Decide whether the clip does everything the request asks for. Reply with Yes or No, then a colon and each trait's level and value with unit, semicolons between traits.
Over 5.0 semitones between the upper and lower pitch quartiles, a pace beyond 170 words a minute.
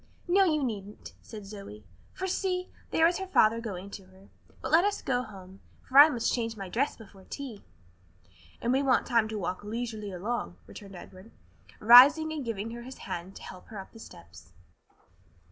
Yes: wide, 5.5 semitones; average, 190 wpm